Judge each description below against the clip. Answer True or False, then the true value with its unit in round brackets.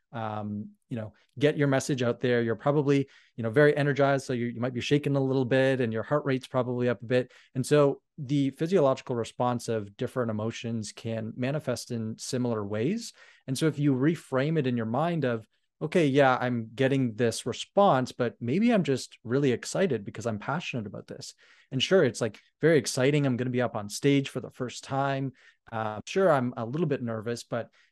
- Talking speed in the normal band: False (210 wpm)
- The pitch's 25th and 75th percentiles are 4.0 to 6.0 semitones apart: False (3.3 semitones)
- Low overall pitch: True (130 Hz)